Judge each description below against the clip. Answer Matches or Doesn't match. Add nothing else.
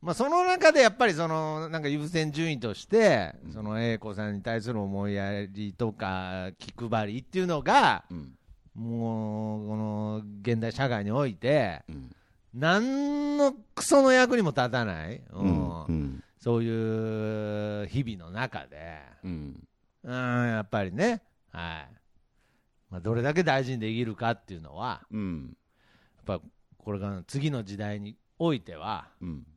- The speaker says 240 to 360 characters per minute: Doesn't match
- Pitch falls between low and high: Doesn't match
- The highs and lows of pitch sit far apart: Matches